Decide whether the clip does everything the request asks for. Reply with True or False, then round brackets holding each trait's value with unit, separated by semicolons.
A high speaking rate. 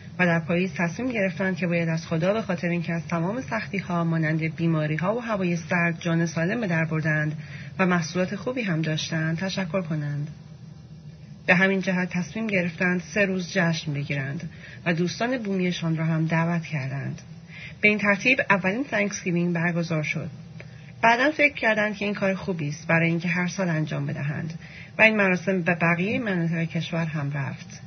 True (170 wpm)